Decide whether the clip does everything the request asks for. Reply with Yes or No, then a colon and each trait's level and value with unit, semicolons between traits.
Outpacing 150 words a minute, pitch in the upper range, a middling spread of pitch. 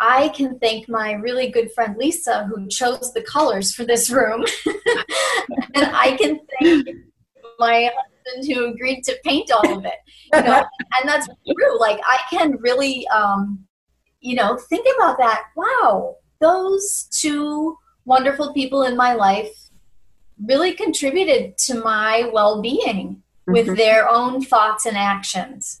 No: average, 145 wpm; very high, 250 Hz; average, 5.0 semitones